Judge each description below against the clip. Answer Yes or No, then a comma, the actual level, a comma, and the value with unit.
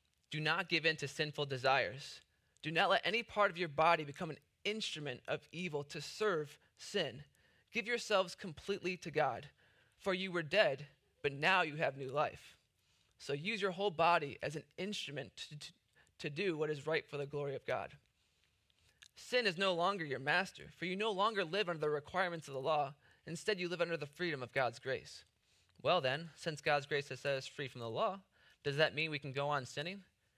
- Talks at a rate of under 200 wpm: No, fast, 205 wpm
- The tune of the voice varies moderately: Yes, average, 4.3 semitones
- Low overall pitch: No, medium, 155 Hz